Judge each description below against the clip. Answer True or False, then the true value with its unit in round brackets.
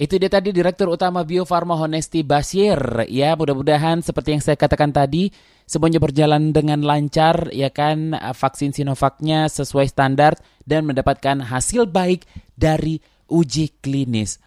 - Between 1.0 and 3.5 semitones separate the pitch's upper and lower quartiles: True (2.9 semitones)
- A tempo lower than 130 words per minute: False (135 wpm)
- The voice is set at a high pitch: False (150 Hz)